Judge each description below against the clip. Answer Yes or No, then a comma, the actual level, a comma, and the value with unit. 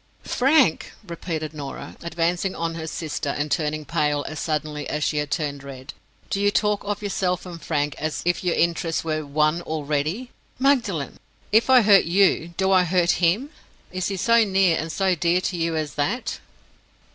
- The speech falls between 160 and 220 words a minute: Yes, average, 180 wpm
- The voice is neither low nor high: Yes, medium, 170 Hz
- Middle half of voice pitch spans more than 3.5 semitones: Yes, average, 4.0 semitones